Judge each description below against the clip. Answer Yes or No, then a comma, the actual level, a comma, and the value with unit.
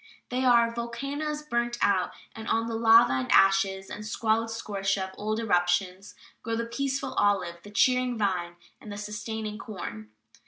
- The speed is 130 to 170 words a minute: Yes, average, 160 wpm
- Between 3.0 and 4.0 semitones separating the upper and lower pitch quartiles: Yes, average, 3.3 semitones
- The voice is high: Yes, high, 215 Hz